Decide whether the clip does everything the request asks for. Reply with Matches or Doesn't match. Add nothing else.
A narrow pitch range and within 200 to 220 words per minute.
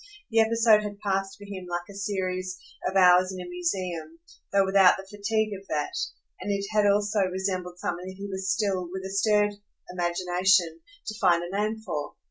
Doesn't match